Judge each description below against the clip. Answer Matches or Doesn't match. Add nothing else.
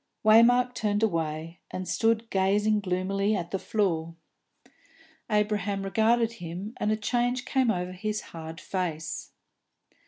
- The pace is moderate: Doesn't match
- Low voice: Doesn't match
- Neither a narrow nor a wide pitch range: Matches